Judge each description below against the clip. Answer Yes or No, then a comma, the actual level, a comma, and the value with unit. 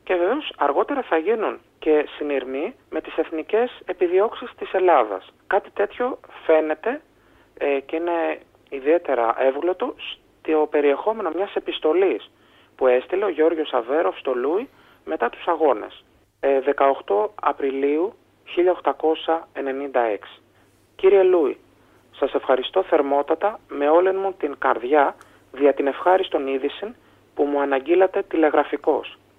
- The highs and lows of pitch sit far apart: Yes, wide, 6.1 semitones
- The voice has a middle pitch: Yes, medium, 155 Hz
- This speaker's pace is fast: No, slow, 115 wpm